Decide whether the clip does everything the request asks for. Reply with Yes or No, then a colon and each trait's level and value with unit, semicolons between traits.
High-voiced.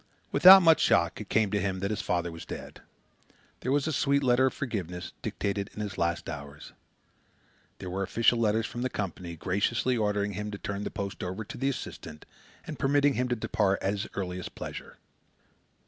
No: low, 105 Hz